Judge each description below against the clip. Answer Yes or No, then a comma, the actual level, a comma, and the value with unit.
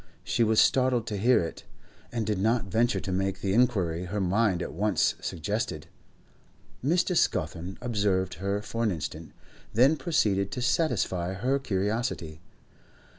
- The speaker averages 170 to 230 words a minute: No, average, 145 wpm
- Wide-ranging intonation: No, average, 4.3 semitones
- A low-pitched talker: Yes, low, 105 Hz